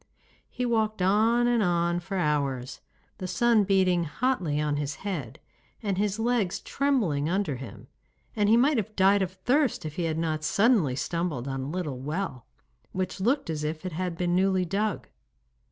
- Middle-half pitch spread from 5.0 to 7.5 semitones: Yes, wide, 5.6 semitones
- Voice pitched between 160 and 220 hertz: Yes, medium, 185 Hz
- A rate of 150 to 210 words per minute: Yes, average, 175 wpm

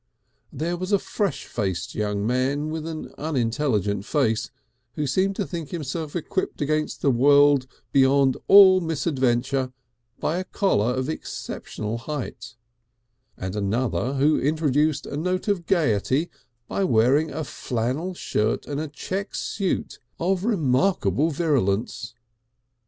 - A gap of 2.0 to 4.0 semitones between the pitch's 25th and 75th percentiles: No, average, 5.0 semitones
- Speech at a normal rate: No, slow, 130 wpm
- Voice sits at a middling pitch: Yes, medium, 145 Hz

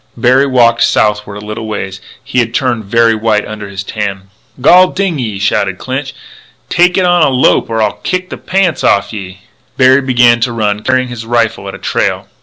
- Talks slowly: No, average, 200 wpm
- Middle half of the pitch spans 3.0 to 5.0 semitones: Yes, average, 3.9 semitones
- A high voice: No, low, 115 Hz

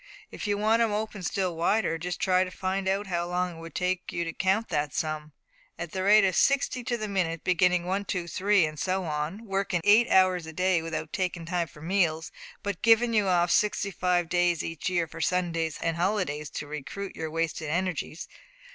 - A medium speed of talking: No, fast, 210 wpm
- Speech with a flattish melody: No, average, 3.1 semitones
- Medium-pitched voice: Yes, medium, 180 Hz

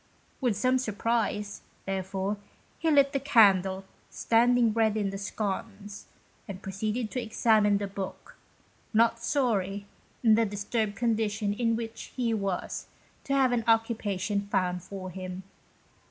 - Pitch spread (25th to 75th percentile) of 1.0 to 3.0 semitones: Yes, average, 2.7 semitones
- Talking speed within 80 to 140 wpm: Yes, slow, 135 wpm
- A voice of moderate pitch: No, high, 215 Hz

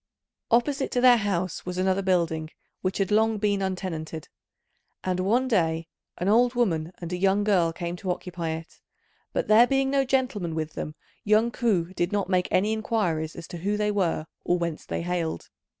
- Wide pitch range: No, average, 4.2 semitones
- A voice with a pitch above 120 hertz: Yes, medium, 185 Hz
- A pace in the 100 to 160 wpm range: No, average, 185 wpm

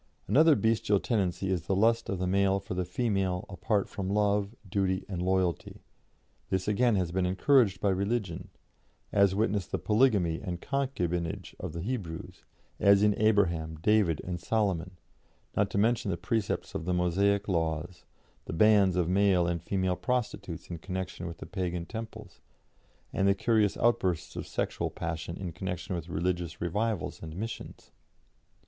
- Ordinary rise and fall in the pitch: Yes, average, 3.0 semitones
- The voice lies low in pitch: Yes, very low, 95 Hz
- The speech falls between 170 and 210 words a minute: No, average, 155 wpm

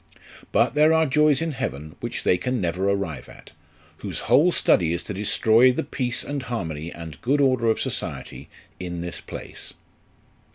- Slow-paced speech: No, average, 170 wpm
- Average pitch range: No, wide, 7.9 semitones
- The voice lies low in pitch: Yes, low, 115 Hz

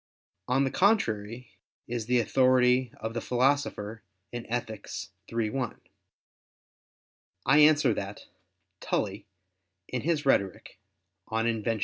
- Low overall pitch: Yes, low, 120 Hz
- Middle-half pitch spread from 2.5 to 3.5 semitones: Yes, average, 3.1 semitones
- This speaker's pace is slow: Yes, slow, 110 wpm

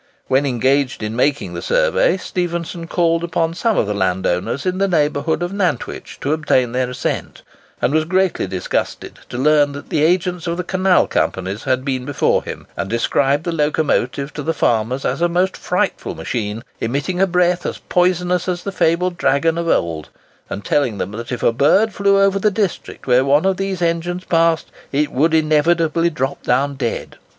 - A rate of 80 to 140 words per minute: No, average, 185 wpm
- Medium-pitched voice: Yes, medium, 155 Hz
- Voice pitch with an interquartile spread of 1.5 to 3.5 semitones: No, wide, 5.4 semitones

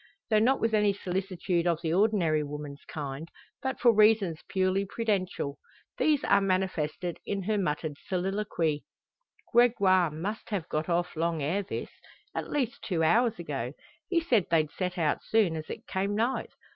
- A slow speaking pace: No, average, 160 wpm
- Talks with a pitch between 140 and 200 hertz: Yes, medium, 185 Hz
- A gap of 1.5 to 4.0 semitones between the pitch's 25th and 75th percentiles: No, average, 4.7 semitones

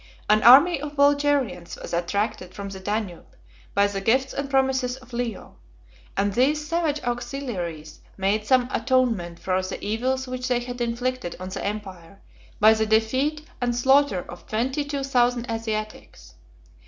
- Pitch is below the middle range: No, high, 240 Hz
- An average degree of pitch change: Yes, average, 4.7 semitones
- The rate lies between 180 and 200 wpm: No, average, 155 wpm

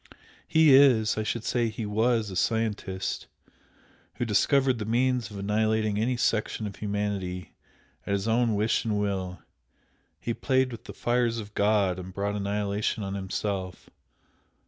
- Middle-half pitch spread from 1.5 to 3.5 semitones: Yes, narrow, 2.6 semitones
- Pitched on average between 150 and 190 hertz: No, low, 105 Hz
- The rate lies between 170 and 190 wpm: No, average, 150 wpm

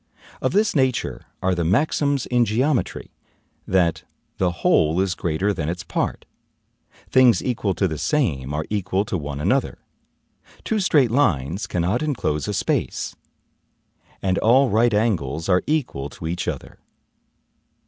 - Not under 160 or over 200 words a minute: No, average, 140 wpm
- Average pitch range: No, wide, 7.2 semitones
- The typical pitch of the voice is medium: No, very low, 95 Hz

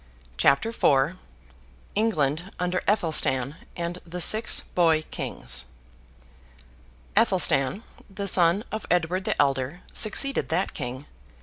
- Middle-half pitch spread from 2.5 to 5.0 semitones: No, wide, 5.5 semitones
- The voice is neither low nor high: Yes, medium, 170 Hz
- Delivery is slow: Yes, slow, 105 wpm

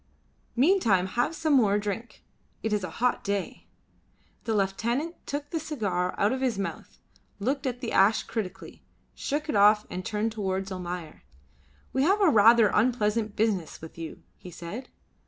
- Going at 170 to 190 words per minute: No, average, 160 wpm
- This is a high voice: Yes, high, 215 Hz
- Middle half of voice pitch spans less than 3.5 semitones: No, average, 4.7 semitones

